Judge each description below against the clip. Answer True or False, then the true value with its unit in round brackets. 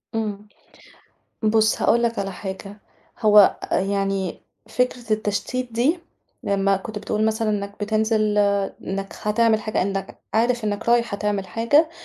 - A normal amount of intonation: False (2.3 semitones)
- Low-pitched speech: False (215 Hz)